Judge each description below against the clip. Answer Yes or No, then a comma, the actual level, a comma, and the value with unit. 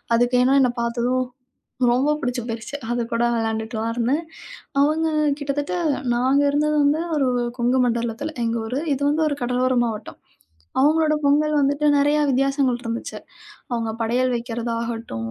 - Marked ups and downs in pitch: No, average, 3.6 semitones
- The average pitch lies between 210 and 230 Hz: No, very high, 250 Hz